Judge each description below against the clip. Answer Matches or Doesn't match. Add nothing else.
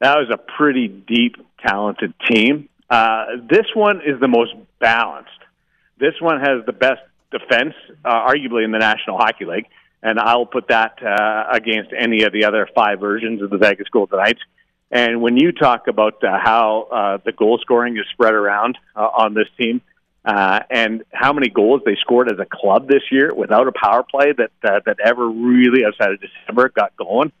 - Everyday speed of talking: Matches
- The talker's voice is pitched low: Matches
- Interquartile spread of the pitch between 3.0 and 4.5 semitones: Doesn't match